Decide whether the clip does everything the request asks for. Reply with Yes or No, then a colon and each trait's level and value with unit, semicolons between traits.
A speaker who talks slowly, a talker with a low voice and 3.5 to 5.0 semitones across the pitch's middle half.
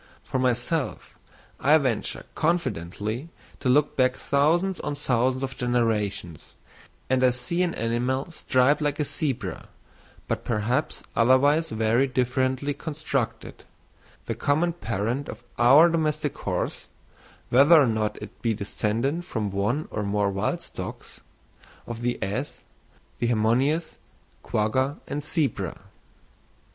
Yes: slow, 125 wpm; low, 130 Hz; average, 4.4 semitones